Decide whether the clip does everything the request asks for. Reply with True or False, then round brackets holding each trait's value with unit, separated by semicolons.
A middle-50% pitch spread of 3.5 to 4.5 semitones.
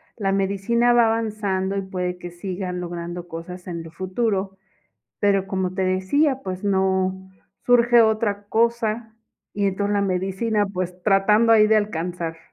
False (2.7 semitones)